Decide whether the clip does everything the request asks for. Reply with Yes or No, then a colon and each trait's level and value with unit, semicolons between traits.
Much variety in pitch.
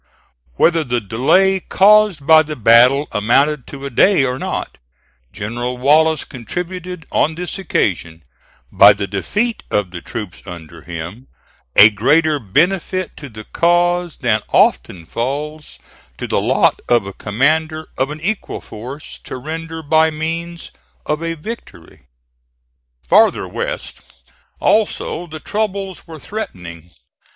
Yes: wide, 7.1 semitones